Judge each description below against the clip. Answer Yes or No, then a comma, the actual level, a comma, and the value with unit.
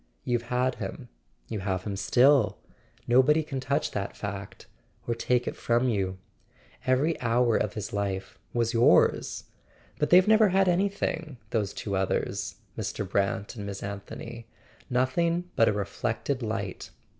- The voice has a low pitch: Yes, low, 115 Hz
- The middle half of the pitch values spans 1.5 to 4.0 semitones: No, average, 4.7 semitones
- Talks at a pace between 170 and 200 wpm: No, average, 155 wpm